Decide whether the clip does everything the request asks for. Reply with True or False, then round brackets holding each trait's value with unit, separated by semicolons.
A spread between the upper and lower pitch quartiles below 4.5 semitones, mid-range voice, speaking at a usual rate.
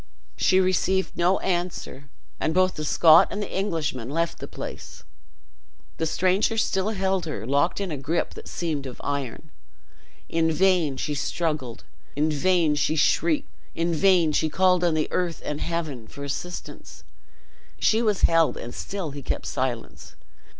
True (4.0 semitones; 165 Hz; 155 wpm)